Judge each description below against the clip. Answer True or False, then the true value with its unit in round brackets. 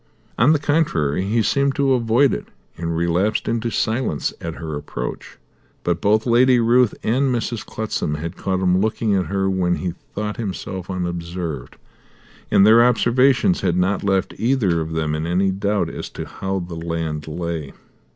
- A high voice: False (95 Hz)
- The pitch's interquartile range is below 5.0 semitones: False (5.5 semitones)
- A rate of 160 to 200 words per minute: True (170 wpm)